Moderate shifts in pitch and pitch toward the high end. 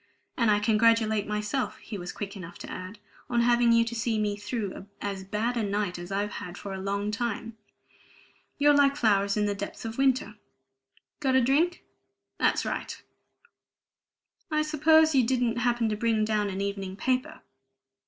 Yes: average, 3.3 semitones; high, 220 Hz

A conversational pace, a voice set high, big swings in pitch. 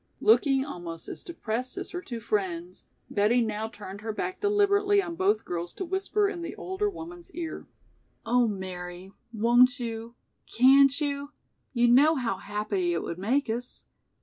Yes: average, 160 wpm; high, 245 Hz; wide, 8.4 semitones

